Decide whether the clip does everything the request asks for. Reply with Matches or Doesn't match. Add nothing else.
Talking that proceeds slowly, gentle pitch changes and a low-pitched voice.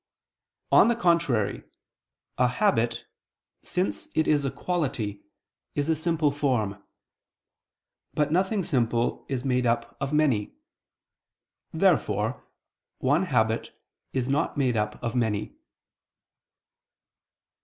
Doesn't match